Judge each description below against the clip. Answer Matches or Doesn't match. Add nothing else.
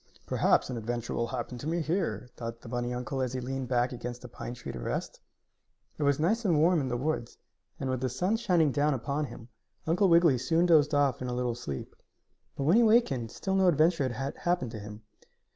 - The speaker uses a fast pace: Matches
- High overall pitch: Doesn't match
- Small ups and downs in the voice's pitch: Doesn't match